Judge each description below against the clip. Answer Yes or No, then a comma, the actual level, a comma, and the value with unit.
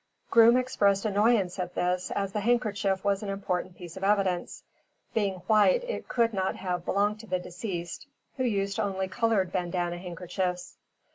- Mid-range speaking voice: No, high, 195 Hz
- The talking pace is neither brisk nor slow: Yes, average, 160 wpm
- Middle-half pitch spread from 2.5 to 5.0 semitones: Yes, average, 2.9 semitones